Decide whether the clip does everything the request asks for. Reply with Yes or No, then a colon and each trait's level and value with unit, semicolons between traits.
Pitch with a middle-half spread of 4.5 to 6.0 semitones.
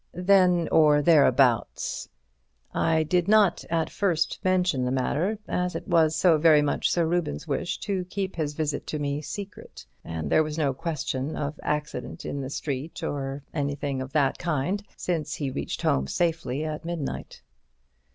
No: average, 3.5 semitones